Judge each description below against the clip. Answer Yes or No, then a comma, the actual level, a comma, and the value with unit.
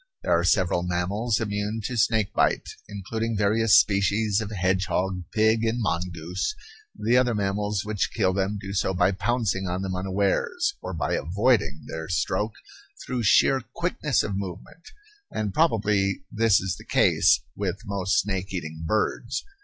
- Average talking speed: Yes, average, 155 wpm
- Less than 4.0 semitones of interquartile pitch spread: Yes, average, 3.1 semitones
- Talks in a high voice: No, low, 100 Hz